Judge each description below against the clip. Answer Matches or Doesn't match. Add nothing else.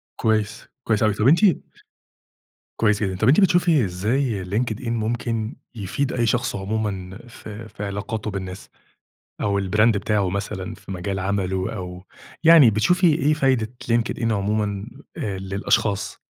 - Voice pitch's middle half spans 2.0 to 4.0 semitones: Matches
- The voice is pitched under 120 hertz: Matches